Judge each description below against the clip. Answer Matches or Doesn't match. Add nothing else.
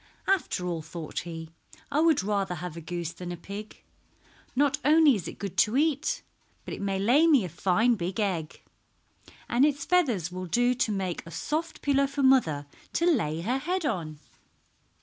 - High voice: Matches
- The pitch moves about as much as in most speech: Doesn't match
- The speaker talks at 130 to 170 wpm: Doesn't match